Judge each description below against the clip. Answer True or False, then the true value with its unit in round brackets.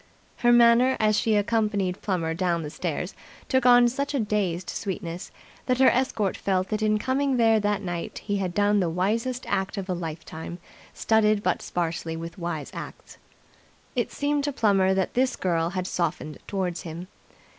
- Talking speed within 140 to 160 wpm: False (175 wpm)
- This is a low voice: False (200 Hz)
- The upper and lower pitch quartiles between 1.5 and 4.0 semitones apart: False (4.6 semitones)